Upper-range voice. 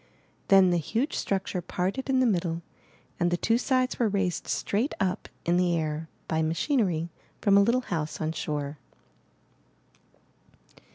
No: medium, 180 Hz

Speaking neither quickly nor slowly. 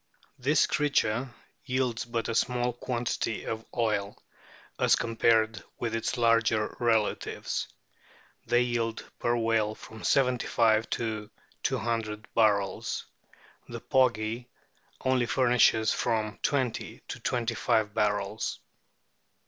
No: slow, 115 wpm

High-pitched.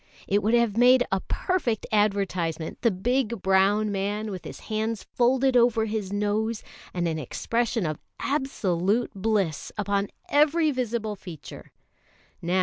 Yes: high, 215 Hz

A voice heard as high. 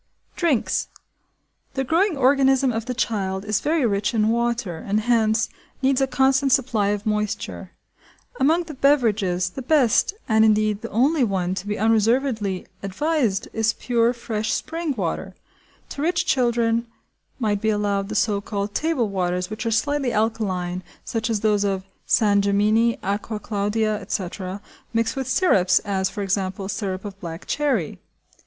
Yes: high, 220 Hz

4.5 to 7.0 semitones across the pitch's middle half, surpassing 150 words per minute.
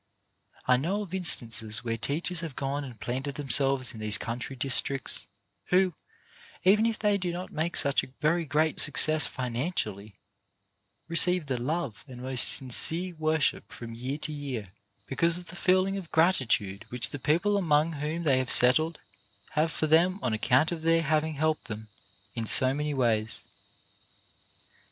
Yes: average, 5.1 semitones; average, 160 wpm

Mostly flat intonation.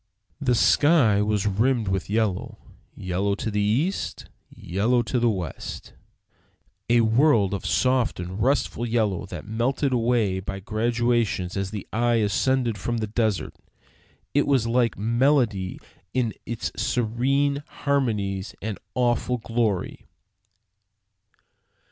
No: average, 3.5 semitones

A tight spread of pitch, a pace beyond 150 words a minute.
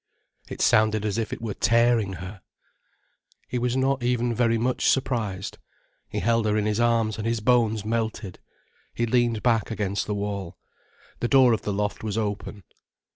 Yes: narrow, 2.3 semitones; average, 175 wpm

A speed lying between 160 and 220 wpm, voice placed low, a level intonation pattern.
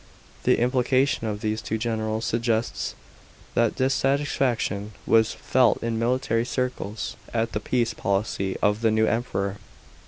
No: slow, 135 wpm; low, 115 Hz; narrow, 2.3 semitones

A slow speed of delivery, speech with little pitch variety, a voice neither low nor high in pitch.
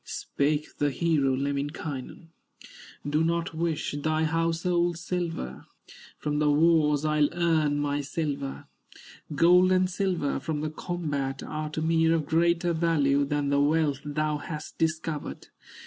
Yes: slow, 130 wpm; narrow, 2.3 semitones; medium, 155 Hz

